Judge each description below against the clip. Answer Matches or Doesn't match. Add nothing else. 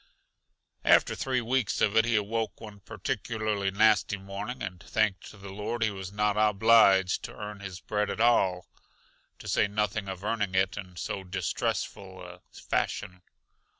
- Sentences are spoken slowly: Doesn't match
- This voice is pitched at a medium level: Doesn't match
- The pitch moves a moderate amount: Doesn't match